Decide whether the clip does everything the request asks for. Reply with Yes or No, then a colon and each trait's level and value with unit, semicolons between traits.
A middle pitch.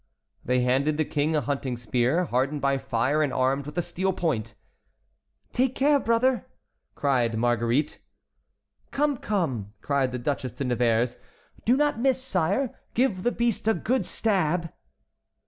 Yes: medium, 150 Hz